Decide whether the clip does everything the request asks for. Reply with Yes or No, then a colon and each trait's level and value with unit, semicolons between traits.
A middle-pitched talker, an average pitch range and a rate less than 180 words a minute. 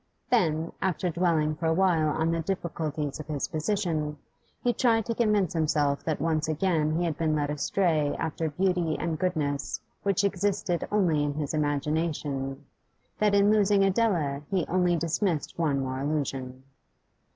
Yes: medium, 160 Hz; average, 3.8 semitones; average, 150 wpm